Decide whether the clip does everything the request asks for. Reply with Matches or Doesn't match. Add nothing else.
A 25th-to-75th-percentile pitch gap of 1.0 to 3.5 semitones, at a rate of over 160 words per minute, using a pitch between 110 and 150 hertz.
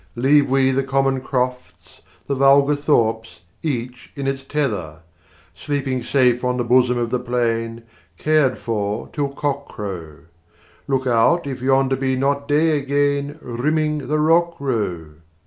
Doesn't match